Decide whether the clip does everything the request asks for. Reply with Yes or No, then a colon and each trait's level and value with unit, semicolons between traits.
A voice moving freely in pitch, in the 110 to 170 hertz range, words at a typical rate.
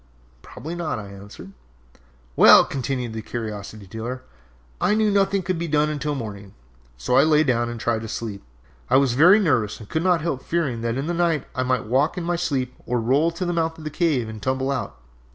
No: wide, 6.2 semitones; low, 135 Hz; fast, 215 wpm